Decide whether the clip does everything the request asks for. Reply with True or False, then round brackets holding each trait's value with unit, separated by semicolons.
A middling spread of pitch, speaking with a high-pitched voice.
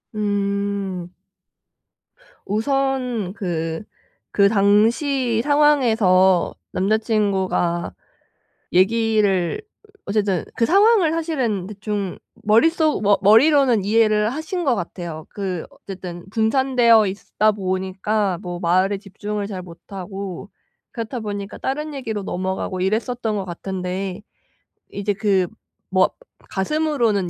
True (3.6 semitones; 205 Hz)